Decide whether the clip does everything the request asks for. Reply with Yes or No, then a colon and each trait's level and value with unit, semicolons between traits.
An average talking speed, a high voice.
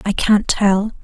Yes: average, 175 wpm; high, 205 Hz